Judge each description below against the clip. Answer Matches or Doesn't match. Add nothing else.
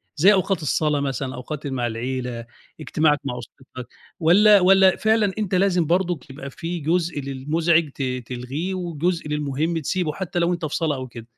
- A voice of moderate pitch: Matches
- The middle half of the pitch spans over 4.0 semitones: Matches